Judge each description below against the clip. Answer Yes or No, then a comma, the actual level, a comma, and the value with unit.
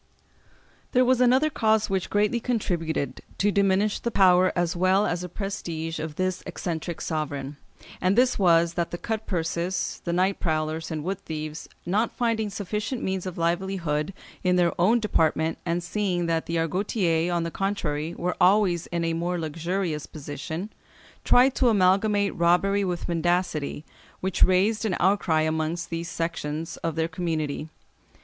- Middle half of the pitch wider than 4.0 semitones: No, average, 3.4 semitones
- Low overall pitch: No, medium, 175 Hz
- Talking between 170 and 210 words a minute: No, average, 160 wpm